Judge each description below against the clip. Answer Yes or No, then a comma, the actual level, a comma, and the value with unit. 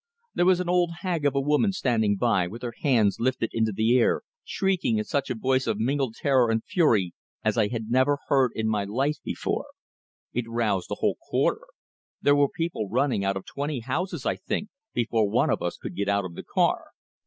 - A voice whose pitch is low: Yes, low, 120 Hz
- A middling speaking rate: No, fast, 210 wpm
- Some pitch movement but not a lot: Yes, average, 4.7 semitones